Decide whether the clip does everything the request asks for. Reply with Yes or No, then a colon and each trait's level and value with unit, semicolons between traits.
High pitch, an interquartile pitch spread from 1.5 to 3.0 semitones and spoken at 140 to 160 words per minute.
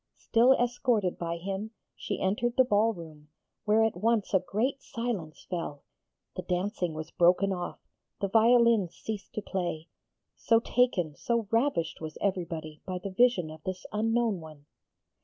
No: high, 195 Hz; average, 5.0 semitones; average, 155 wpm